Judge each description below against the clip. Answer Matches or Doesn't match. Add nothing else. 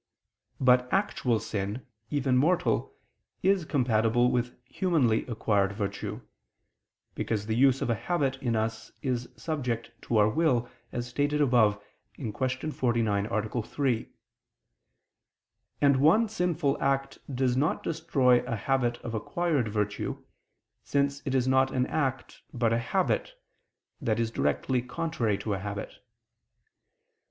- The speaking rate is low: Matches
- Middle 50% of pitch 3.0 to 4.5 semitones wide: Matches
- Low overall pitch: Matches